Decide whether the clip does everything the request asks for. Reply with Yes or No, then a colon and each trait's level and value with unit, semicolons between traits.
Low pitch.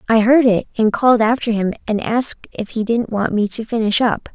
No: high, 225 Hz